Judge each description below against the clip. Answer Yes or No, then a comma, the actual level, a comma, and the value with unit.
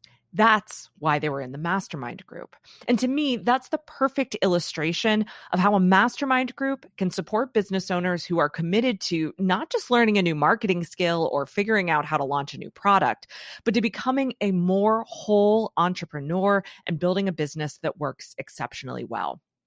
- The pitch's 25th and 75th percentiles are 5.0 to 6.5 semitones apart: Yes, wide, 5.5 semitones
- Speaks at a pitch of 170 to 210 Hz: Yes, high, 190 Hz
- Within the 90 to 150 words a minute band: No, average, 180 wpm